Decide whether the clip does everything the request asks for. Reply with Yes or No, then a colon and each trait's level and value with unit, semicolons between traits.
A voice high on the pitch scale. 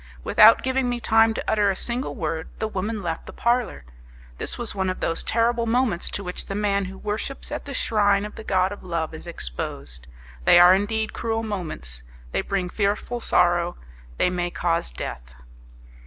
Yes: high, 200 Hz